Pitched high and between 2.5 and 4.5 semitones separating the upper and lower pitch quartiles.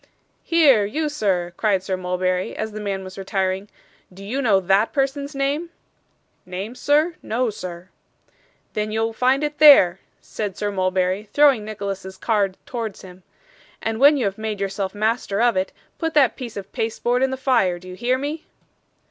No: high, 215 Hz; wide, 5.5 semitones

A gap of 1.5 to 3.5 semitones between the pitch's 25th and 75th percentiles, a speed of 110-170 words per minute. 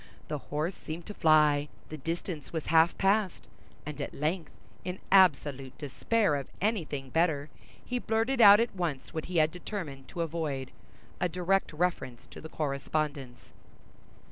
No: average, 4.0 semitones; average, 140 wpm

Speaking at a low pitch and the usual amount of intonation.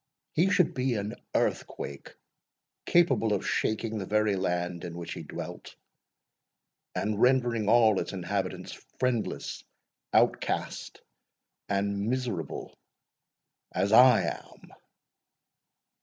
Yes: low, 105 Hz; average, 3.9 semitones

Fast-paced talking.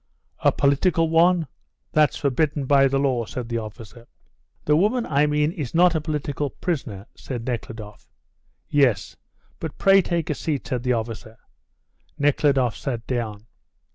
No: average, 145 wpm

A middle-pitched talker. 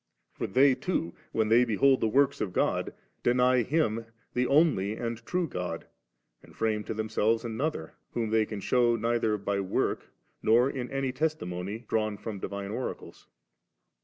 No: low, 115 Hz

